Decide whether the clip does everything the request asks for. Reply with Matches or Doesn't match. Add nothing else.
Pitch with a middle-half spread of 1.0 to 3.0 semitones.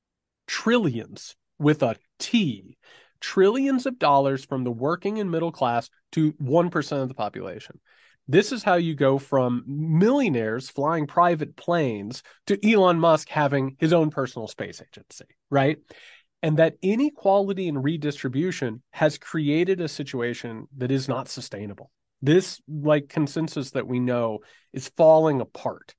Doesn't match